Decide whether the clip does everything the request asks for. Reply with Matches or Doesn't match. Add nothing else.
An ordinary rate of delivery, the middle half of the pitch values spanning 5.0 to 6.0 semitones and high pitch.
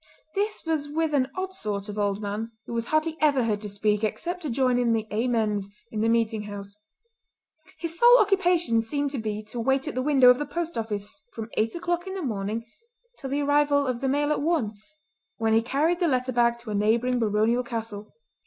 Doesn't match